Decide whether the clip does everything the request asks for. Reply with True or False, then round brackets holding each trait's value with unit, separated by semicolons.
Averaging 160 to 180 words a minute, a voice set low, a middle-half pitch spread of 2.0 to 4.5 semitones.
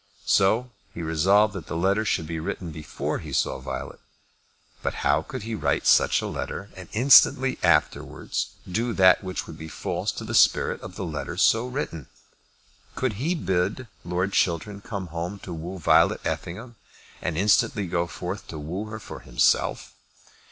True (170 wpm; 95 Hz; 4.2 semitones)